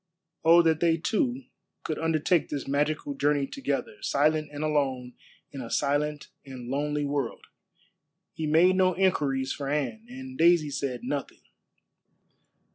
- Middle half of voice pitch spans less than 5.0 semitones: Yes, average, 3.2 semitones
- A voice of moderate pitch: Yes, medium, 150 Hz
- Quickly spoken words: No, slow, 135 wpm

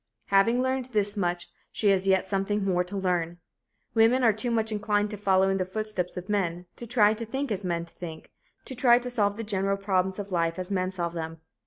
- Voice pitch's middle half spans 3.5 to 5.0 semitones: No, average, 3.0 semitones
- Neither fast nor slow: No, fast, 220 wpm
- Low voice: No, high, 195 Hz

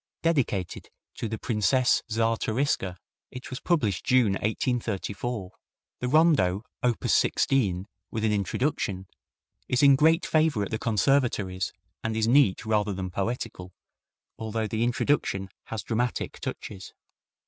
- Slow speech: Yes, slow, 125 wpm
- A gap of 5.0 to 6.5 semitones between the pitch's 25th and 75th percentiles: No, average, 4.3 semitones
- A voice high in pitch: No, low, 110 Hz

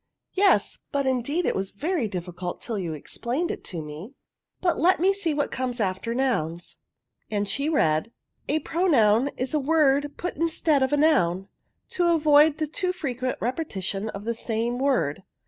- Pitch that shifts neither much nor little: No, wide, 7.4 semitones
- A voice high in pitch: Yes, very high, 260 Hz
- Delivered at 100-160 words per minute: No, average, 185 wpm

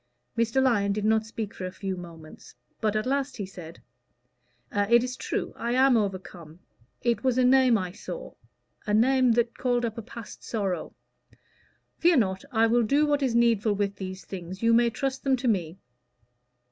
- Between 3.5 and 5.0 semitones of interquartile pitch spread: Yes, average, 4.2 semitones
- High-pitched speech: Yes, high, 225 Hz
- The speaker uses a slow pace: No, average, 185 wpm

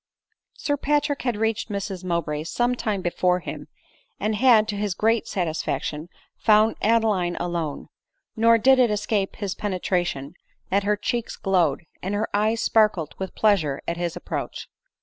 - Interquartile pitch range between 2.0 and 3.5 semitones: No, average, 4.1 semitones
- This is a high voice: Yes, high, 205 Hz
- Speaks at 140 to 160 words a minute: Yes, average, 155 wpm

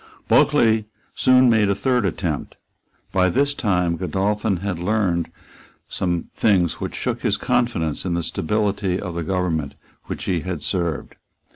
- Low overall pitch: Yes, very low, 95 Hz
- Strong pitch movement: No, average, 3.7 semitones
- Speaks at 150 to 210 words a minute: No, average, 140 wpm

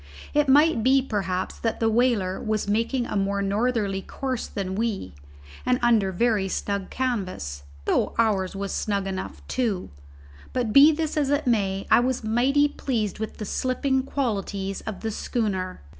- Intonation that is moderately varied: Yes, average, 4.5 semitones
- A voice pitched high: Yes, high, 220 Hz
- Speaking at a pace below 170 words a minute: Yes, average, 160 wpm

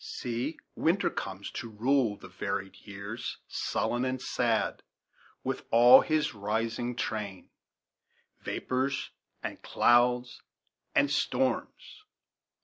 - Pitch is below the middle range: Yes, low, 120 Hz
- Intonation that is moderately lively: Yes, average, 3.4 semitones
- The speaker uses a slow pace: Yes, slow, 100 wpm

